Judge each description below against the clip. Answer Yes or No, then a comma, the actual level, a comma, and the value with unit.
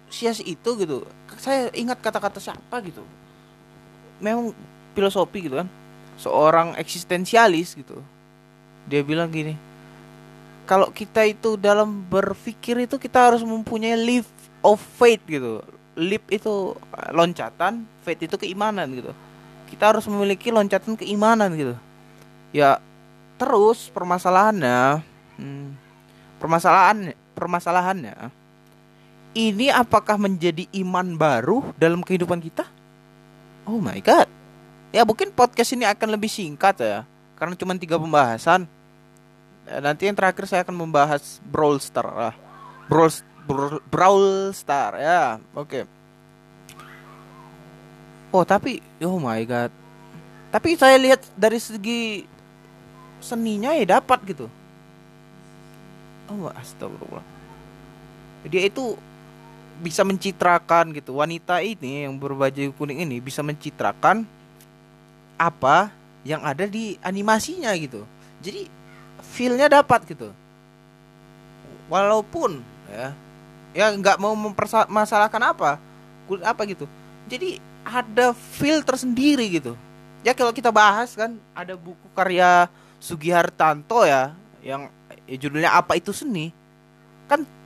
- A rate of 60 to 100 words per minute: No, average, 110 wpm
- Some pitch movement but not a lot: No, wide, 7.6 semitones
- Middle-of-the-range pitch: Yes, medium, 180 Hz